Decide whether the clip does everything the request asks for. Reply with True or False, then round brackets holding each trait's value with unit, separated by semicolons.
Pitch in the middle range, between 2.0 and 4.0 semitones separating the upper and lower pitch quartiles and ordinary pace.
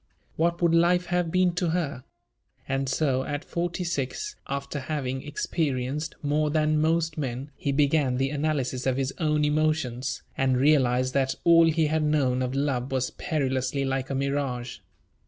True (145 Hz; 3.1 semitones; 160 wpm)